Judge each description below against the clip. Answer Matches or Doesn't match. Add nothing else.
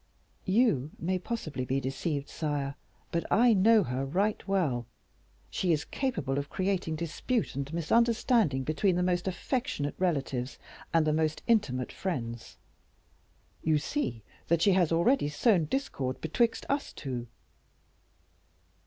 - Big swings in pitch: Matches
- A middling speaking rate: Doesn't match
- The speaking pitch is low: Doesn't match